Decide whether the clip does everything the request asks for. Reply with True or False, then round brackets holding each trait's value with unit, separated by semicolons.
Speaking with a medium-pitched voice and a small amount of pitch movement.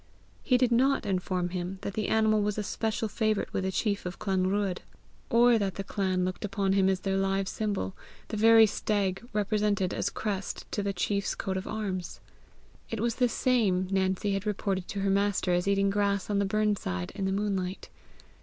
False (200 Hz; 2.0 semitones)